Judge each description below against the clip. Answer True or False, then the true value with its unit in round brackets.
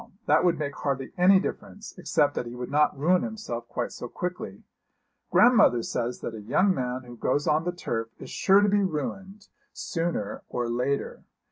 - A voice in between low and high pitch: True (150 Hz)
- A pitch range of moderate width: False (7.0 semitones)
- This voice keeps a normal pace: True (180 wpm)